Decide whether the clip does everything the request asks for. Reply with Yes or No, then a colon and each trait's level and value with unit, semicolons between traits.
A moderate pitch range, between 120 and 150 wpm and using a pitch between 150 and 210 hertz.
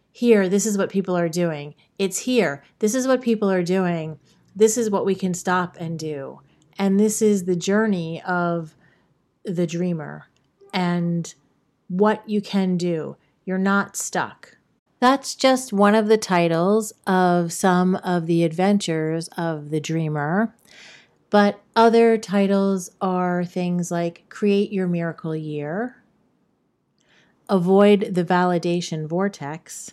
Yes: average, 3.4 semitones; slow, 135 wpm; medium, 185 Hz